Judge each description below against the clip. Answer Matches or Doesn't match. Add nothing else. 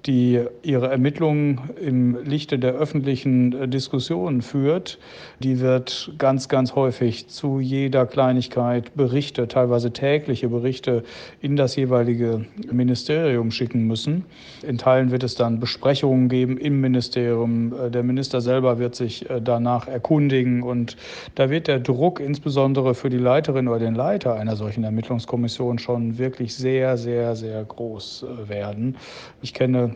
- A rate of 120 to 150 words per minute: Matches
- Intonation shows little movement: Matches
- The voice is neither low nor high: Doesn't match